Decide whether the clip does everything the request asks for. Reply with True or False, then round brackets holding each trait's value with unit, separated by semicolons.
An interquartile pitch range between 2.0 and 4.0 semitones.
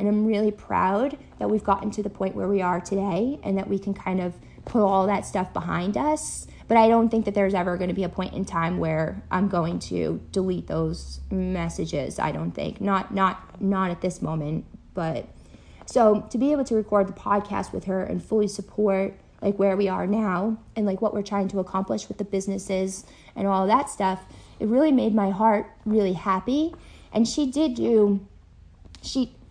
True (2.5 semitones)